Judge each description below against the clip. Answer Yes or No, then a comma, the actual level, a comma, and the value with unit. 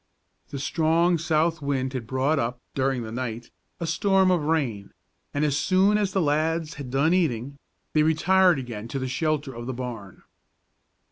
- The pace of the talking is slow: No, average, 175 wpm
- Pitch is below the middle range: No, medium, 145 Hz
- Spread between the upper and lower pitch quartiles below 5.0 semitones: Yes, average, 4.4 semitones